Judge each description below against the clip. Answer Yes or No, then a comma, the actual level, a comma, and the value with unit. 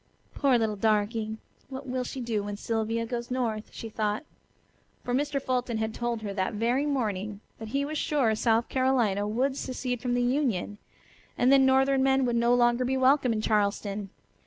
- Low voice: No, high, 240 Hz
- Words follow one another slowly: No, average, 180 wpm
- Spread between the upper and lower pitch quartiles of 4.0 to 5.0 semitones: No, average, 3.3 semitones